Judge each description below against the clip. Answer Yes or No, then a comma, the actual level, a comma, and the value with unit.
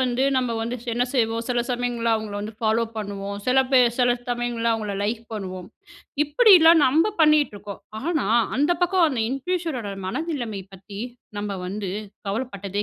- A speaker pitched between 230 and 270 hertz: Yes, high, 240 Hz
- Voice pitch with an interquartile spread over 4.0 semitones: Yes, average, 4.7 semitones